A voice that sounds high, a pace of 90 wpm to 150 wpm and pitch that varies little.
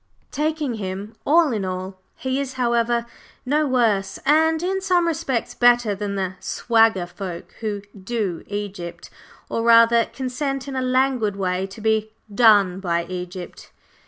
No: high, 225 Hz; average, 145 wpm; average, 5.2 semitones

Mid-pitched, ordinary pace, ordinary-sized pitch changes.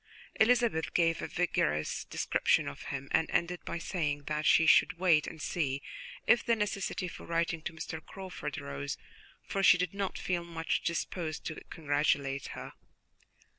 Yes: medium, 165 Hz; average, 160 wpm; average, 3.4 semitones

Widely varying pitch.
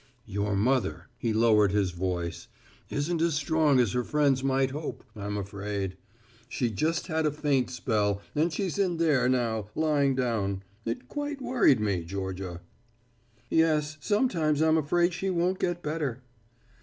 Yes: wide, 7.4 semitones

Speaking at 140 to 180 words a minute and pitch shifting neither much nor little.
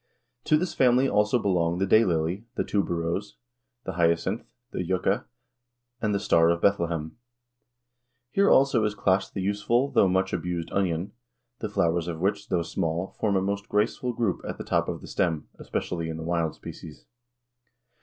Yes: average, 170 wpm; average, 3.8 semitones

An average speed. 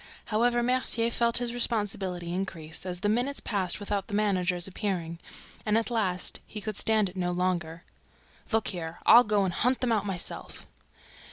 Yes: average, 170 wpm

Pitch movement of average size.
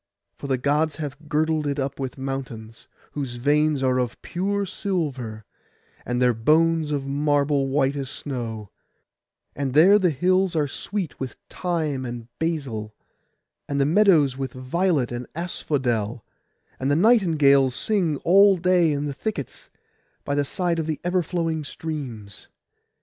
Yes: average, 4.1 semitones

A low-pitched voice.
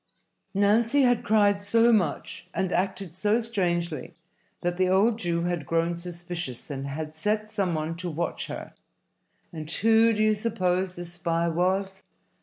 No: medium, 185 Hz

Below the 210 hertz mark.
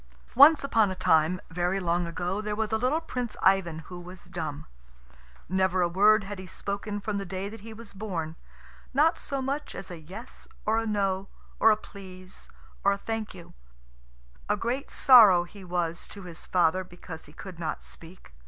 Yes: high, 190 Hz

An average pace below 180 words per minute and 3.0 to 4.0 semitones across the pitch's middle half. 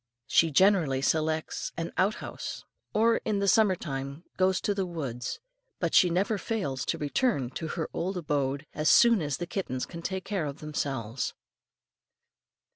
No: average, 165 wpm; wide, 5.5 semitones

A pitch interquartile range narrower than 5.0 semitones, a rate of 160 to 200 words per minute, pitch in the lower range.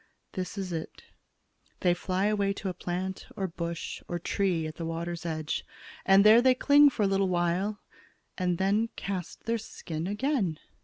No: average, 3.1 semitones; average, 170 wpm; high, 190 Hz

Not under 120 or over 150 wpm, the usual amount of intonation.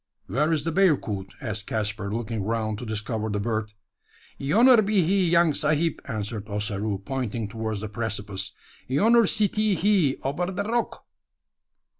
No: average, 145 wpm; wide, 8.3 semitones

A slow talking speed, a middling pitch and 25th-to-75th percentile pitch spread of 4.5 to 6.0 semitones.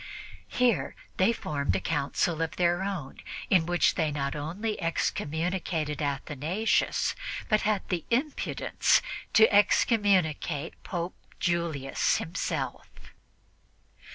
Yes: slow, 100 wpm; medium, 170 Hz; average, 4.8 semitones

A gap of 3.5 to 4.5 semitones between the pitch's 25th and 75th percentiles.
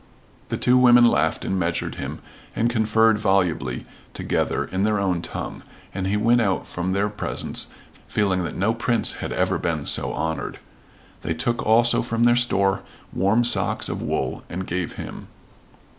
Yes: average, 3.9 semitones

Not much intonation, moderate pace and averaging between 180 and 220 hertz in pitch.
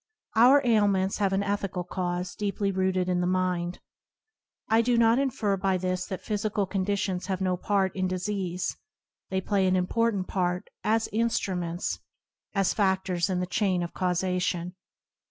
Yes: narrow, 2.0 semitones; average, 155 wpm; high, 190 Hz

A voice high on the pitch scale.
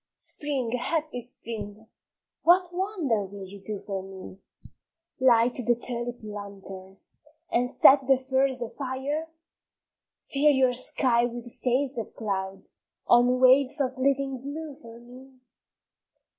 Yes: very high, 250 Hz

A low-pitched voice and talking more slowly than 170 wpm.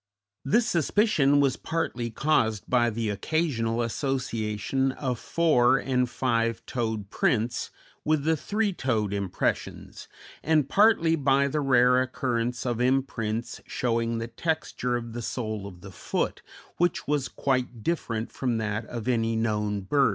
Yes: low, 125 Hz; average, 140 wpm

